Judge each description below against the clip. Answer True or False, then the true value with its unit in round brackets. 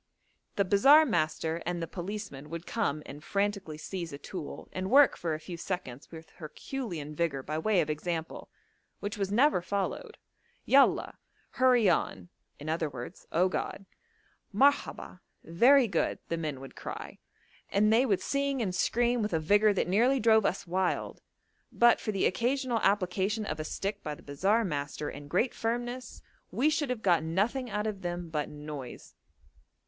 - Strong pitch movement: True (6.0 semitones)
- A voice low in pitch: False (190 Hz)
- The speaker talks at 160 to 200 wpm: True (165 wpm)